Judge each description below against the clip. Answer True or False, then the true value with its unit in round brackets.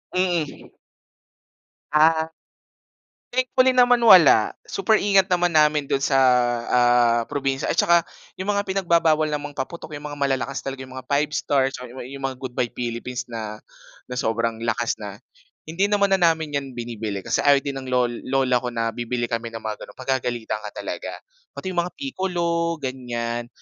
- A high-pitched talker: False (140 Hz)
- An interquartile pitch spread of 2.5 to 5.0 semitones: False (5.6 semitones)